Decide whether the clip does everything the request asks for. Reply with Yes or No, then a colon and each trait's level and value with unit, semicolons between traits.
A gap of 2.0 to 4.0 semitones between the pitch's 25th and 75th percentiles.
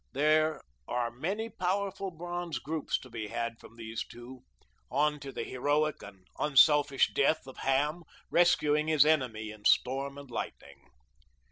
No: average, 4.5 semitones